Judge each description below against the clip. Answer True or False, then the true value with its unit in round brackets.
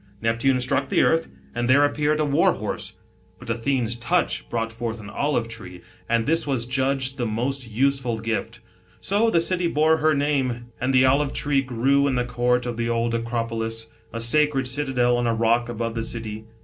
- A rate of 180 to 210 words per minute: True (190 wpm)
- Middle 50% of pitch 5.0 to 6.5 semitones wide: False (3.3 semitones)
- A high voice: False (125 Hz)